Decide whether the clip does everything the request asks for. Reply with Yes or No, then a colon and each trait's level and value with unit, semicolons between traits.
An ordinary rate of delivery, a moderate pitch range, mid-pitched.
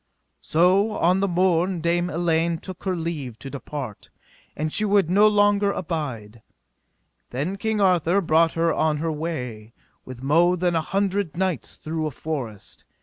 Yes: average, 155 wpm; average, 3.7 semitones; medium, 165 Hz